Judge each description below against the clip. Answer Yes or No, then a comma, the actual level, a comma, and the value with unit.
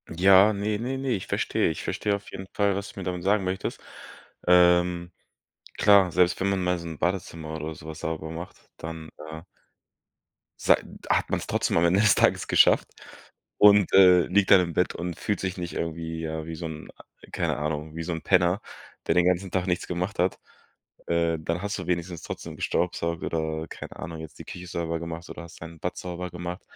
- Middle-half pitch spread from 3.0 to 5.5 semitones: No, narrow, 2.4 semitones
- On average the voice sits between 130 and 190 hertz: No, very low, 90 Hz